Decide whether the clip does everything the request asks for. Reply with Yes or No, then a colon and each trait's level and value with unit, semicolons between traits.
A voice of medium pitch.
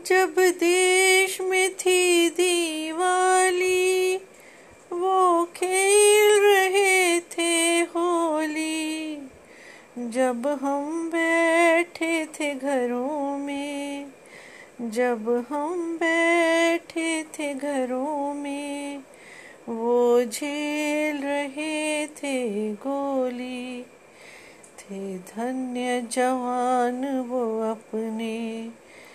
No: very high, 305 Hz